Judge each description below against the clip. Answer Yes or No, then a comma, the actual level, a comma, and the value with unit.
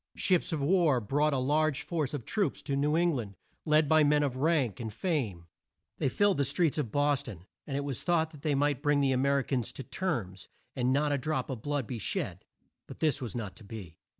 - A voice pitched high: No, medium, 140 Hz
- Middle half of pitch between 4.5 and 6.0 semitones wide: No, average, 3.6 semitones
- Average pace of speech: No, fast, 230 wpm